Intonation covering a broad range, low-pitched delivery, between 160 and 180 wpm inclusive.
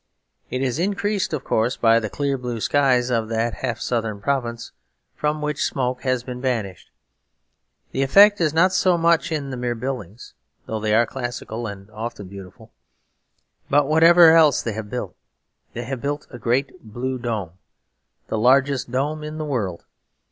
No: average, 4.3 semitones; low, 125 Hz; average, 170 wpm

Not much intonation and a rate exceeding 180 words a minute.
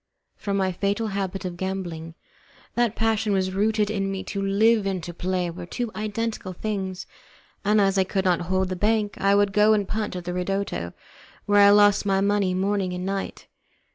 Yes: narrow, 1.9 semitones; average, 200 wpm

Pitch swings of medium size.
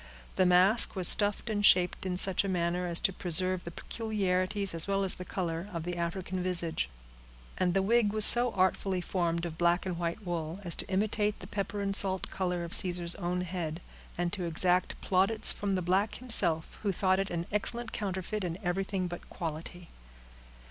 No: narrow, 2.2 semitones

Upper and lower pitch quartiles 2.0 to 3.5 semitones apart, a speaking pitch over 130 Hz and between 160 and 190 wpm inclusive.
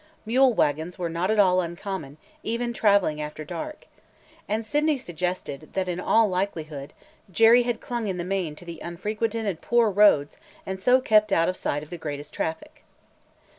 No: average, 5.2 semitones; medium, 185 Hz; average, 170 wpm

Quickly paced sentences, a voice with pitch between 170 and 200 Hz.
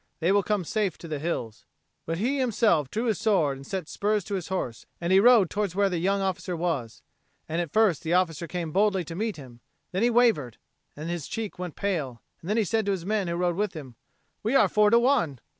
Yes: fast, 235 wpm; medium, 185 Hz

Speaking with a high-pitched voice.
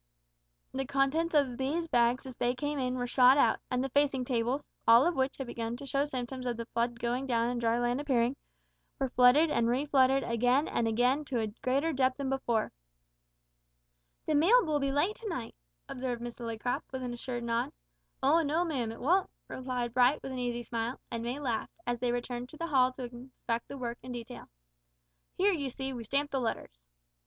Yes: very high, 255 Hz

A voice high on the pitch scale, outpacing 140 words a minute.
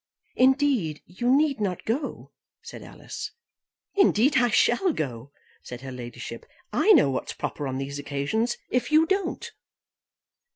No: high, 225 Hz; slow, 135 wpm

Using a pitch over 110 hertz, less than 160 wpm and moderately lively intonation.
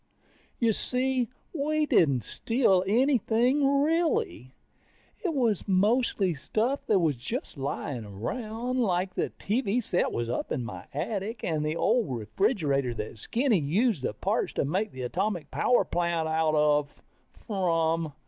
No: high, 190 Hz; average, 140 wpm; wide, 8.5 semitones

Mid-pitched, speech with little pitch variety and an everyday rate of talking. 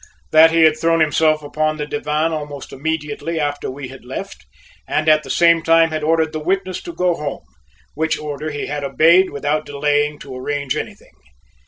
Yes: medium, 155 Hz; narrow, 2.0 semitones; average, 185 wpm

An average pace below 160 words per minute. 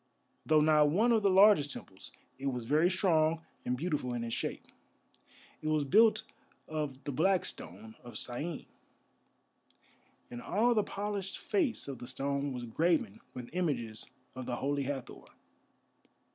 Yes: average, 150 wpm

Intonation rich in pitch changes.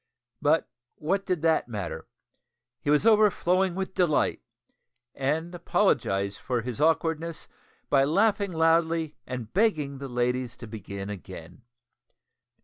Yes: wide, 6.0 semitones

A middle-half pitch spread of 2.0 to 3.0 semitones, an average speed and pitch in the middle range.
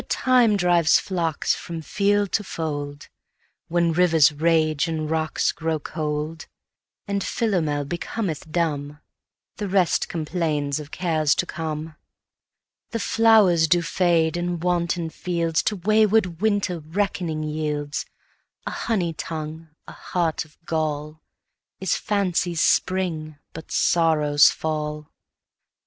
No: average, 2.7 semitones; slow, 120 wpm; medium, 165 Hz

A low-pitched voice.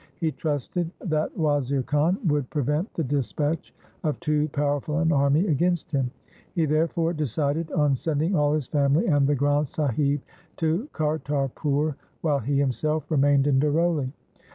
No: medium, 150 Hz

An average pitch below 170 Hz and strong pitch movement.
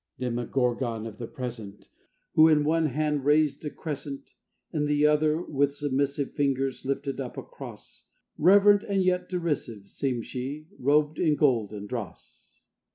No: medium, 140 Hz; average, 3.4 semitones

